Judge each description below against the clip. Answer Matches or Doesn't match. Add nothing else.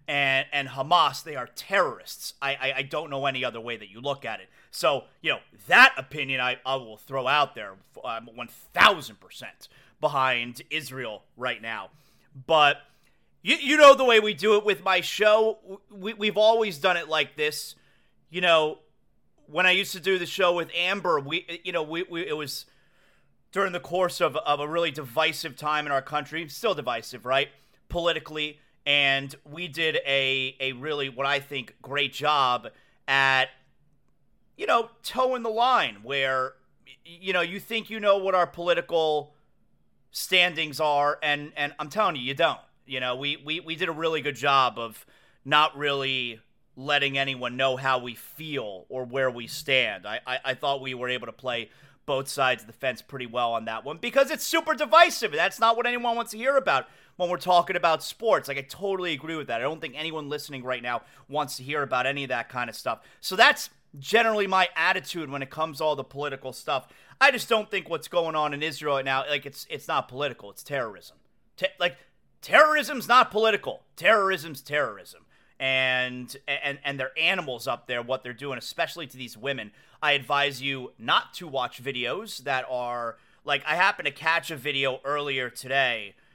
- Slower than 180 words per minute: Doesn't match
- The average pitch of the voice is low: Doesn't match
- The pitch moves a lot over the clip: Doesn't match